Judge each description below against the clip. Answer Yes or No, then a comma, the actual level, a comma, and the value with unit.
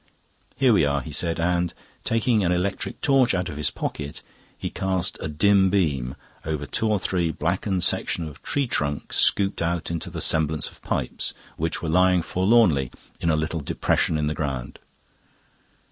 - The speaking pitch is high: No, very low, 85 Hz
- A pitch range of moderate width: Yes, average, 4.0 semitones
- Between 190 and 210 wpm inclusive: No, average, 175 wpm